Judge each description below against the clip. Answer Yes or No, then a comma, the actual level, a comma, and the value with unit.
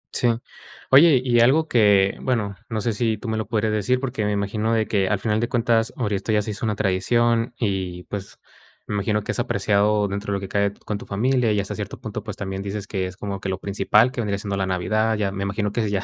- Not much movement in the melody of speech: Yes, narrow, 2.3 semitones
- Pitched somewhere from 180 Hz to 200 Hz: No, low, 105 Hz